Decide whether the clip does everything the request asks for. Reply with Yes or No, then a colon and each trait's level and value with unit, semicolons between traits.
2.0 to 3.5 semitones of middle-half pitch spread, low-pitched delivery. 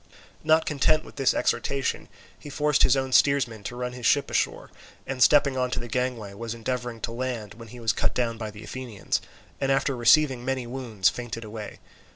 Yes: average, 2.8 semitones; low, 125 Hz